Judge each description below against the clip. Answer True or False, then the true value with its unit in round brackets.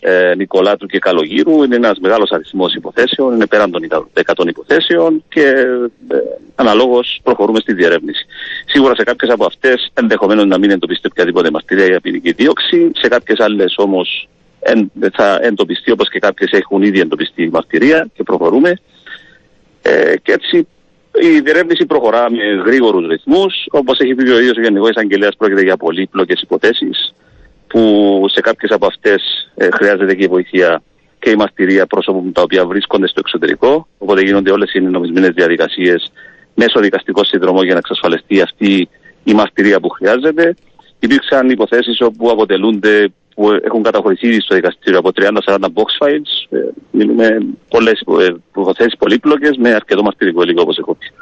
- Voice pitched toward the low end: True (125 Hz)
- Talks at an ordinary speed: True (155 wpm)